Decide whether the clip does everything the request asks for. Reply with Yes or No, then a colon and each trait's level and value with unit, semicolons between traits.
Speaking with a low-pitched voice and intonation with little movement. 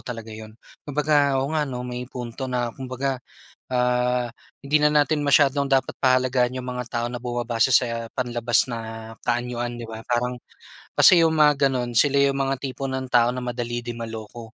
Yes: low, 125 Hz; narrow, 2.3 semitones